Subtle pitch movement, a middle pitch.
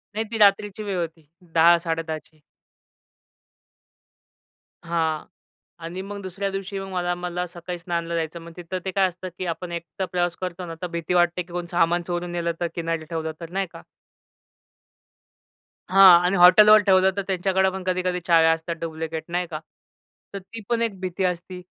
Yes: narrow, 2.0 semitones; medium, 175 Hz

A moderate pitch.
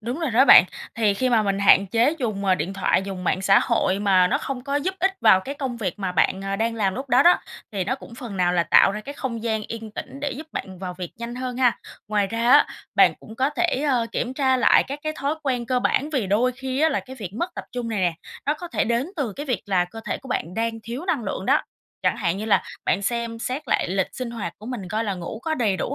No: high, 230 Hz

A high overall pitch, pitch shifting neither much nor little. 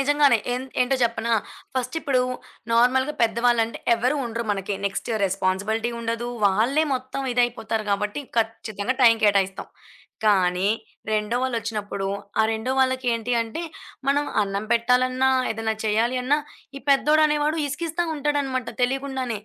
Yes: high, 235 Hz; average, 3.3 semitones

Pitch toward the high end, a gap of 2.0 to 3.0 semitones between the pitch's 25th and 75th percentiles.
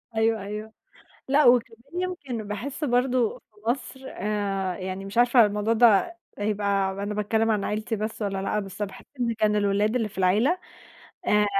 Yes: high, 215 Hz; average, 2.7 semitones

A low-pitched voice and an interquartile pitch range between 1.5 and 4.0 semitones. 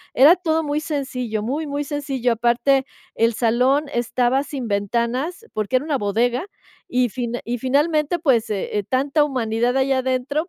No: very high, 260 Hz; average, 3.5 semitones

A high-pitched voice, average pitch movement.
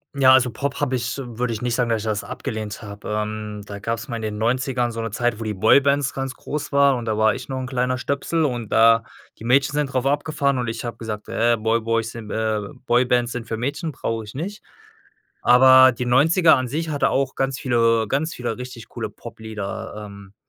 No: low, 120 Hz; average, 3.2 semitones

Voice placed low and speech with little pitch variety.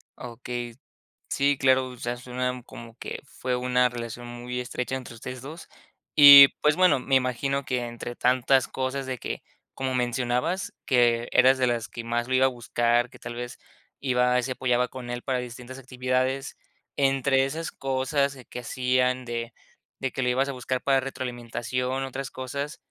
Yes: low, 125 Hz; narrow, 1.5 semitones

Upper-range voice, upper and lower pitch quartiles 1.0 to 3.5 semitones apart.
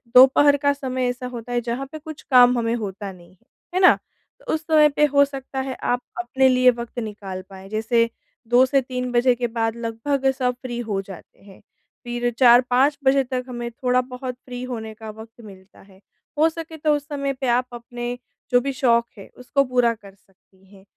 Yes: high, 245 Hz; average, 2.8 semitones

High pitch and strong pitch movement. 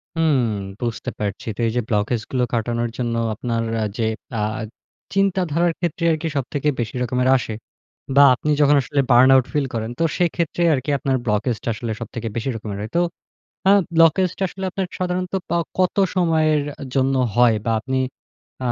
No: low, 135 Hz; wide, 5.9 semitones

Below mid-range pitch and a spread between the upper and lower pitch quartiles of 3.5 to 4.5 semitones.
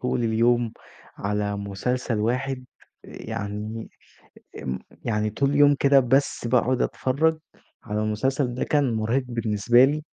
Yes: low, 120 Hz; average, 3.8 semitones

